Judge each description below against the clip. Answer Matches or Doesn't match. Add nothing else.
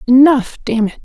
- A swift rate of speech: Doesn't match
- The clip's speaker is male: Doesn't match